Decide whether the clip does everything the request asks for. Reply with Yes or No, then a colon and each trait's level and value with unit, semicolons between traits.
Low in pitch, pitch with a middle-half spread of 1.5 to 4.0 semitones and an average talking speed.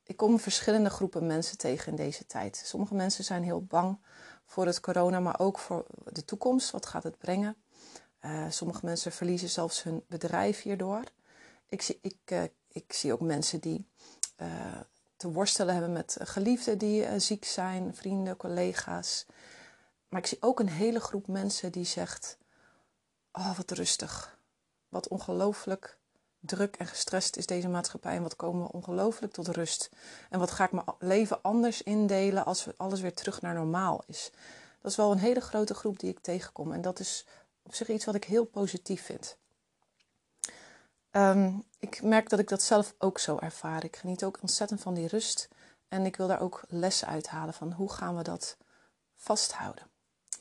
No: high, 190 Hz; average, 3.1 semitones; average, 180 wpm